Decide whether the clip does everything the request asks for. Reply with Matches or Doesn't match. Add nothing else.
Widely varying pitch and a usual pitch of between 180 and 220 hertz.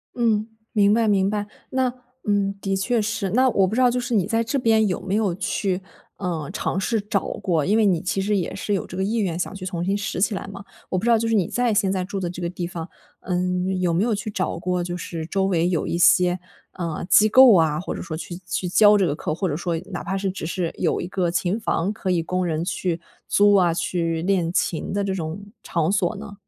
Doesn't match